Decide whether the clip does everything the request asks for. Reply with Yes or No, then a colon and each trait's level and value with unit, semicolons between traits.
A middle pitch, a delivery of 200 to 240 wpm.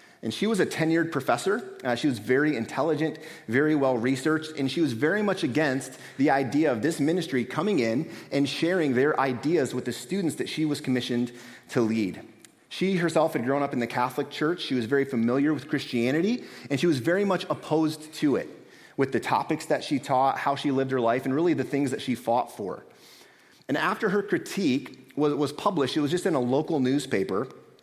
Yes: medium, 145 Hz; fast, 205 wpm